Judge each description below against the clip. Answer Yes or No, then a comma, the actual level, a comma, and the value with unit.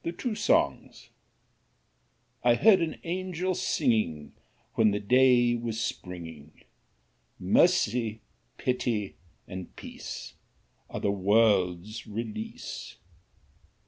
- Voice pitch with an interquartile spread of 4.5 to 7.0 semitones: Yes, wide, 5.4 semitones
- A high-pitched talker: No, low, 110 Hz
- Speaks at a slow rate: Yes, slow, 70 wpm